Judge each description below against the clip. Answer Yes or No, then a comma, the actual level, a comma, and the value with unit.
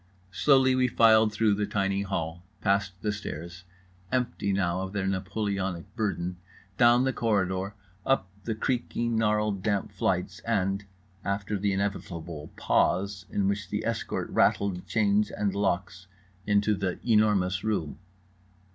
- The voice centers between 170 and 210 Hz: No, low, 100 Hz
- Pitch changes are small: Yes, narrow, 2.3 semitones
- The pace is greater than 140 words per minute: No, slow, 135 wpm